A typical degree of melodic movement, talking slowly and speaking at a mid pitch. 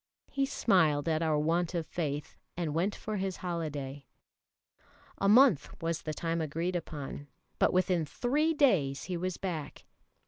No: average, 3.7 semitones; average, 150 wpm; medium, 170 Hz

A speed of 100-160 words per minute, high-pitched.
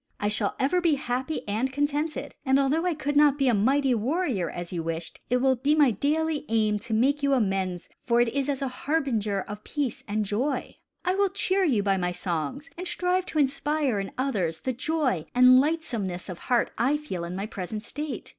No: fast, 205 wpm; very high, 260 Hz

